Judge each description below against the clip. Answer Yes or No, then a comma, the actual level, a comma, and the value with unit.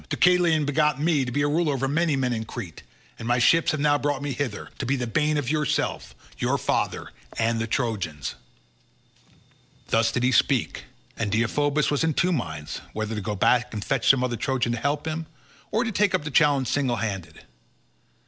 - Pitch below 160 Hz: Yes, low, 135 Hz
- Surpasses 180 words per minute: Yes, average, 200 wpm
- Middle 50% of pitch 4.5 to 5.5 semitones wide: Yes, average, 4.8 semitones